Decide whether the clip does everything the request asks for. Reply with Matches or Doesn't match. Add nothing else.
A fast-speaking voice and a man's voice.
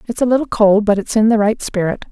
Doesn't match